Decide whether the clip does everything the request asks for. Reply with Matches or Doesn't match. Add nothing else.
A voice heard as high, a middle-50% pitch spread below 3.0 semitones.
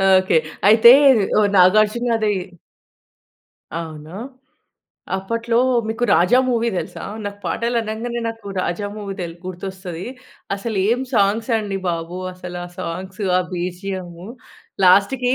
Doesn't match